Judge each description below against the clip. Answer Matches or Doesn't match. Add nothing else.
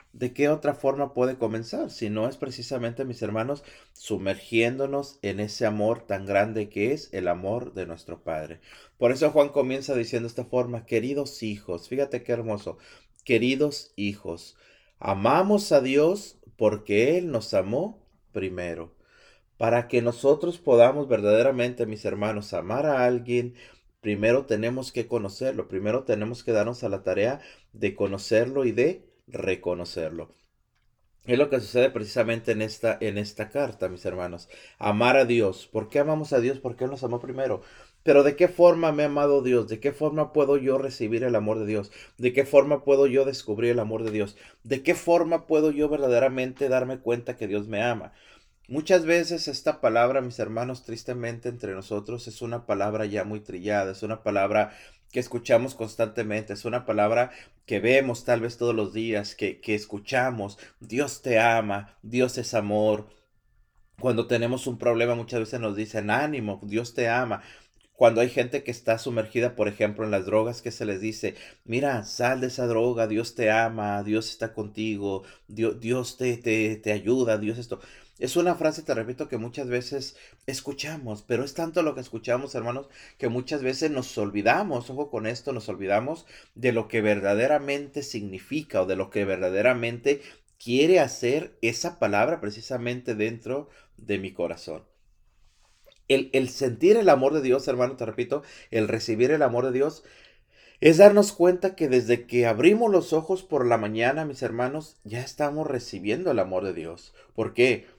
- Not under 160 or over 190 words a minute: Matches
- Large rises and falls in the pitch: Doesn't match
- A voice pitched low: Matches